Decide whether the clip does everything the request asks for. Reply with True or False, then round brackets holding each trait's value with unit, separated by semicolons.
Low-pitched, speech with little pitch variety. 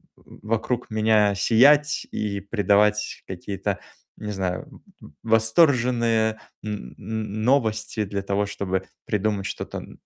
True (110 Hz; 1.9 semitones)